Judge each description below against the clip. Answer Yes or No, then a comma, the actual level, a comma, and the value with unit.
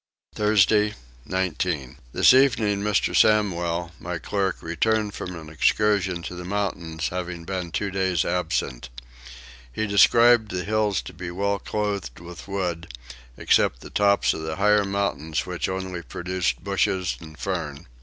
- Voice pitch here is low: Yes, very low, 90 Hz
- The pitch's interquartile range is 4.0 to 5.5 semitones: No, average, 3.2 semitones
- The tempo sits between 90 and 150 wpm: Yes, average, 145 wpm